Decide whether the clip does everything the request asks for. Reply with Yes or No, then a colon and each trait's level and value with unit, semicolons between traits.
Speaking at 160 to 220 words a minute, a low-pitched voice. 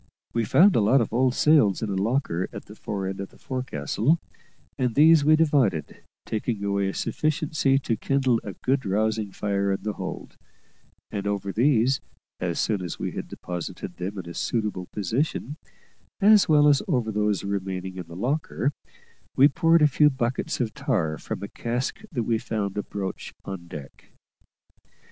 Yes: average, 170 wpm; low, 110 Hz